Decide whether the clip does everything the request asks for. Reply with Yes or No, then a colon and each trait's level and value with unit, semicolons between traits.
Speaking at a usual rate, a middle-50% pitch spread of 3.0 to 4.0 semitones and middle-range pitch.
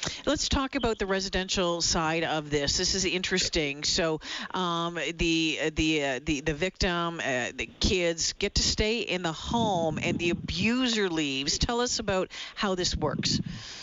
Yes: average, 165 wpm; average, 3.3 semitones; medium, 175 Hz